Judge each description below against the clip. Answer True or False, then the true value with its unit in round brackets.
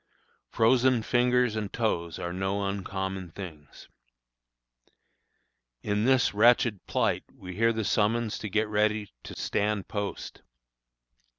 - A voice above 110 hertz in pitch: False (105 Hz)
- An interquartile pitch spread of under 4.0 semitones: True (3.0 semitones)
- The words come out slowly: True (115 wpm)